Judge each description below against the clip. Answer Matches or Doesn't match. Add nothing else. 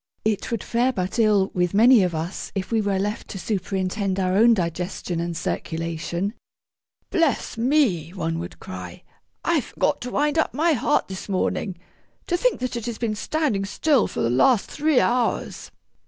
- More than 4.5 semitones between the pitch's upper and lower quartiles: Matches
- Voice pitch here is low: Doesn't match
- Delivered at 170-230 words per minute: Matches